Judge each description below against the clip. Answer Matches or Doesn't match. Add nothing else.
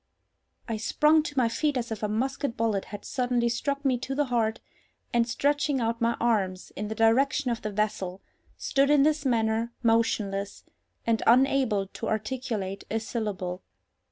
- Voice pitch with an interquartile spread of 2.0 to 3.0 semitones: Doesn't match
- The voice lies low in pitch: Doesn't match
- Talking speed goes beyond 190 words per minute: Doesn't match